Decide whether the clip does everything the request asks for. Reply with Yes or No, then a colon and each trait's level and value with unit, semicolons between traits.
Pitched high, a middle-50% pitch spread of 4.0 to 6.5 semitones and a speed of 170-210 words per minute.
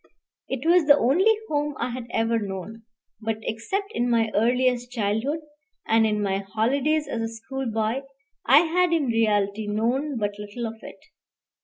No: high, 230 Hz; average, 4.4 semitones; average, 160 wpm